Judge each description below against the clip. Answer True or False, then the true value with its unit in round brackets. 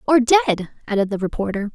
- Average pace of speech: True (170 wpm)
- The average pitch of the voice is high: True (225 Hz)